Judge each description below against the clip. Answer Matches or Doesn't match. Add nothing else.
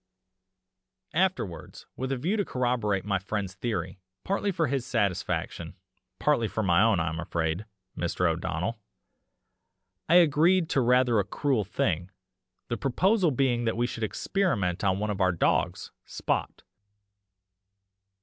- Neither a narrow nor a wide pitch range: Doesn't match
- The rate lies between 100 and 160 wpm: Matches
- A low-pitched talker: Matches